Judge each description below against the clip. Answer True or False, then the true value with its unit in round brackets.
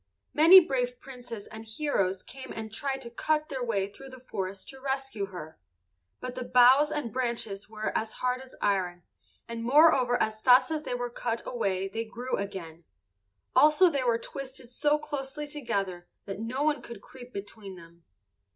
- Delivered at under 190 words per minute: True (175 wpm)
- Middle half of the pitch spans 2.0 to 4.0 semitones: False (4.7 semitones)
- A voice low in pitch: False (245 Hz)